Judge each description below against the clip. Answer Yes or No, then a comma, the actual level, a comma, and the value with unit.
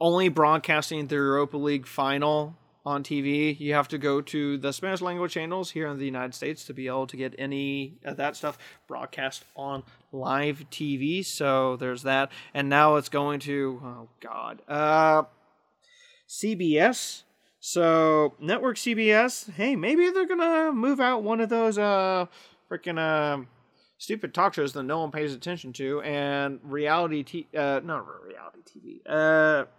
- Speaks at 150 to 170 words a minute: Yes, average, 160 wpm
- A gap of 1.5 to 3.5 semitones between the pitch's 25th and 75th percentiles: No, average, 4.0 semitones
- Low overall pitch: No, medium, 150 Hz